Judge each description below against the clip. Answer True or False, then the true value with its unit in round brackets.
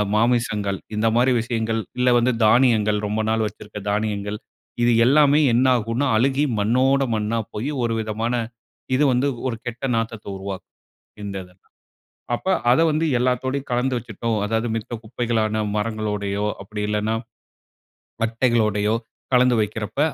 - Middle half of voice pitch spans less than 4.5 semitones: True (2.8 semitones)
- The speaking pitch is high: False (115 Hz)